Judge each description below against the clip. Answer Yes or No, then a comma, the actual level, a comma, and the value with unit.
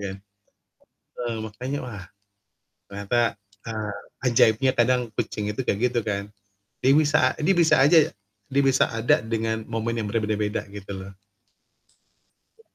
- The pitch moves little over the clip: No, average, 3.3 semitones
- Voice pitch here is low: Yes, low, 115 Hz